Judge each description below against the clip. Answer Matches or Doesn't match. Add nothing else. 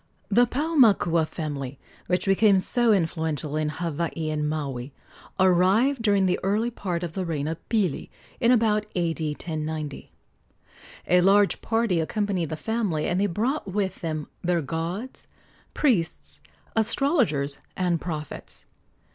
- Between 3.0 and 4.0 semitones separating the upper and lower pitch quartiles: Doesn't match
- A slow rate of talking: Matches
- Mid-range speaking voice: Matches